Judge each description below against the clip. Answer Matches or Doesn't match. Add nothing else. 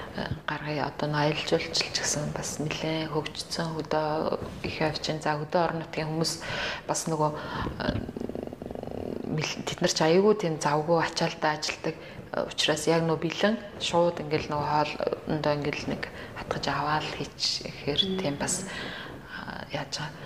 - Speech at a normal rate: Doesn't match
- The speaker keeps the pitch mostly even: Matches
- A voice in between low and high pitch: Matches